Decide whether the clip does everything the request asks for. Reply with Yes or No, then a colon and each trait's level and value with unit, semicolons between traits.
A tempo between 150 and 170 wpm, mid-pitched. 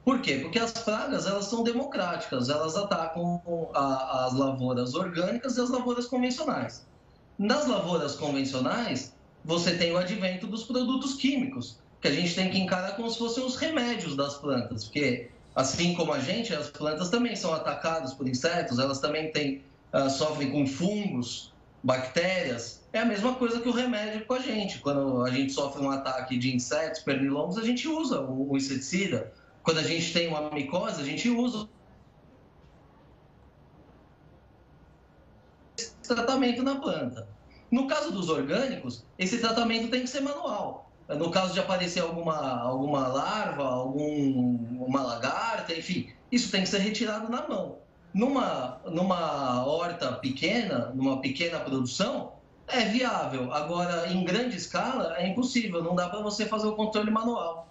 Yes: average, 155 wpm; medium, 175 Hz